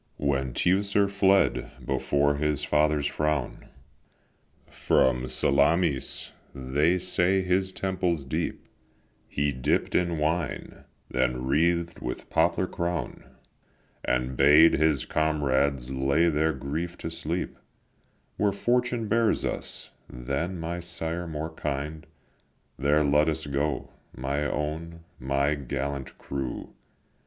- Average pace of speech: No, slow, 110 wpm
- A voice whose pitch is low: Yes, very low, 75 Hz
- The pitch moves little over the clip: No, average, 3.8 semitones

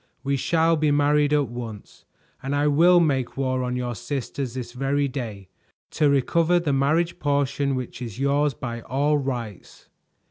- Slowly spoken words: No, average, 165 wpm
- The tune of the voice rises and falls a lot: No, average, 2.8 semitones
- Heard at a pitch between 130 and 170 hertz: Yes, medium, 140 Hz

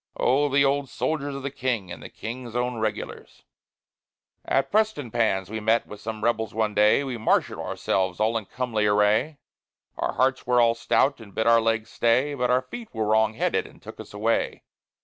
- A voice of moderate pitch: No, low, 115 Hz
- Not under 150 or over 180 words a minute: No, average, 190 wpm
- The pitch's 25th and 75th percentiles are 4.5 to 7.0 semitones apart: No, average, 3.3 semitones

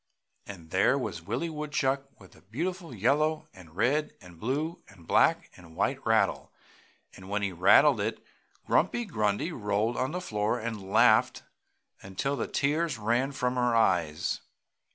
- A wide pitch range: Yes, wide, 6.5 semitones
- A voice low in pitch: Yes, low, 115 Hz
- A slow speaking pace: No, average, 155 wpm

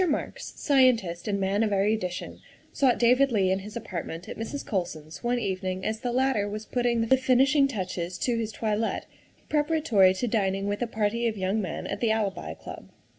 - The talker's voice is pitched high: Yes, high, 215 Hz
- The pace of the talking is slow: No, average, 185 wpm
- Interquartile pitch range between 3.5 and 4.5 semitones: Yes, average, 4.2 semitones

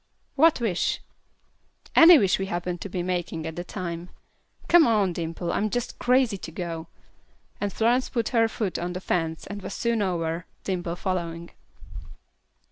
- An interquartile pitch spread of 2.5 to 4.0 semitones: No, average, 4.8 semitones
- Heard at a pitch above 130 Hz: Yes, medium, 185 Hz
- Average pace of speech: Yes, average, 165 wpm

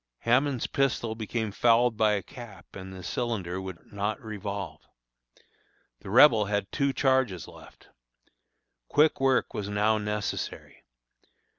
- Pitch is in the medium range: No, low, 110 Hz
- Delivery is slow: Yes, slow, 125 wpm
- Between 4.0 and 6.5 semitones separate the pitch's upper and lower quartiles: No, average, 3.5 semitones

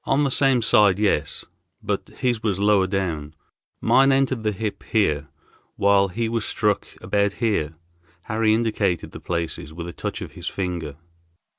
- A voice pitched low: Yes, low, 100 Hz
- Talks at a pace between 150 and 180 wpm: Yes, average, 160 wpm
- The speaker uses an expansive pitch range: No, average, 4.3 semitones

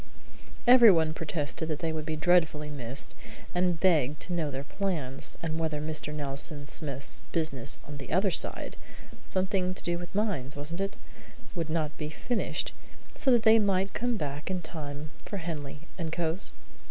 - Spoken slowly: No, average, 165 wpm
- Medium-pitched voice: Yes, medium, 160 Hz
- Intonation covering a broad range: No, average, 3.8 semitones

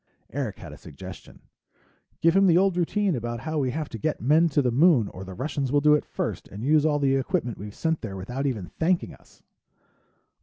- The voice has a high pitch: No, medium, 145 Hz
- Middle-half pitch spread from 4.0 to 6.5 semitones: Yes, average, 5.2 semitones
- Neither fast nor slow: No, fast, 220 wpm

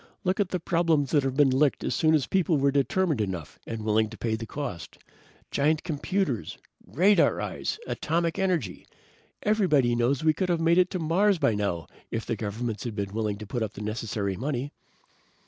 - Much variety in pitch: Yes, wide, 7.3 semitones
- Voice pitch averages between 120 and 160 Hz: Yes, medium, 140 Hz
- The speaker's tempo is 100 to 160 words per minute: No, average, 190 wpm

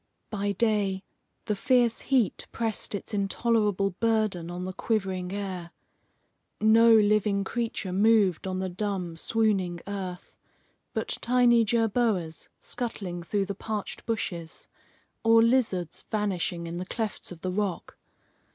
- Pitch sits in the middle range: No, high, 200 Hz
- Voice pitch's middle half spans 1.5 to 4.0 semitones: Yes, average, 3.4 semitones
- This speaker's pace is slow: Yes, slow, 125 wpm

